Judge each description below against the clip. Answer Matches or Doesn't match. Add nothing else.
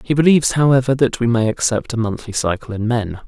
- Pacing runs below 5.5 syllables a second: Doesn't match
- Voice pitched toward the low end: Matches